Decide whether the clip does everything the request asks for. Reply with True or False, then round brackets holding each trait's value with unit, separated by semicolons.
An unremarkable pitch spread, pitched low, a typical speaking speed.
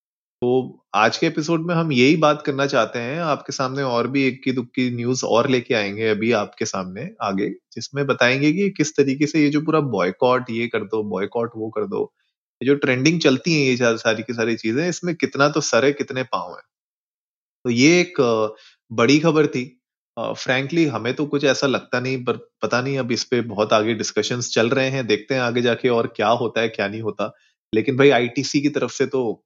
False (3.3 semitones; 130 Hz; 215 wpm)